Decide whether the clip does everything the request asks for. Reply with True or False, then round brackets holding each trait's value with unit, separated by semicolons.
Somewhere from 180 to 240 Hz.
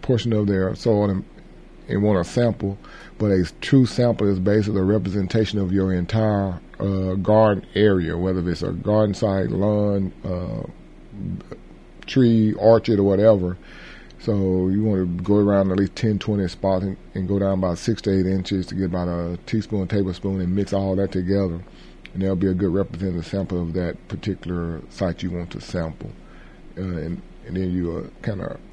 False (95 Hz)